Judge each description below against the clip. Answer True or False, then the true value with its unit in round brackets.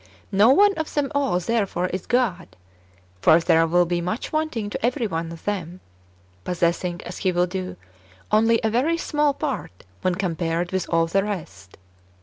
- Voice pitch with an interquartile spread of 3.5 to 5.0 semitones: False (5.5 semitones)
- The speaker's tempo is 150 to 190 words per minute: True (170 wpm)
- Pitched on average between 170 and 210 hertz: True (190 Hz)